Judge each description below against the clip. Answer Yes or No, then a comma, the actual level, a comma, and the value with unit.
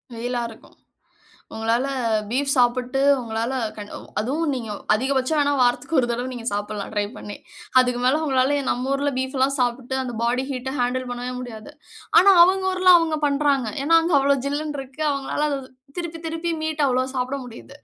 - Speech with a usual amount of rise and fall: Yes, average, 3.0 semitones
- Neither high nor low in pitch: No, very high, 260 Hz